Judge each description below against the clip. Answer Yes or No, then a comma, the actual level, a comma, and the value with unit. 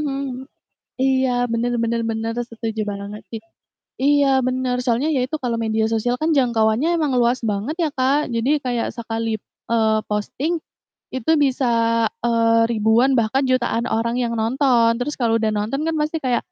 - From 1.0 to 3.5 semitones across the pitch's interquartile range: Yes, average, 2.8 semitones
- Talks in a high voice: Yes, high, 240 Hz